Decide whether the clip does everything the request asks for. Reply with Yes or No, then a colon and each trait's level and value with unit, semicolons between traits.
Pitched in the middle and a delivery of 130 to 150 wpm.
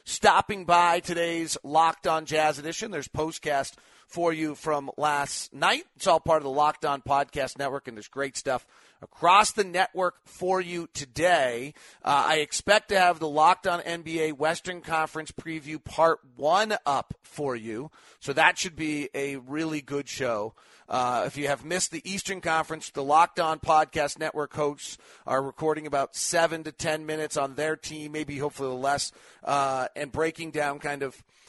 No: medium, 155 Hz; average, 175 wpm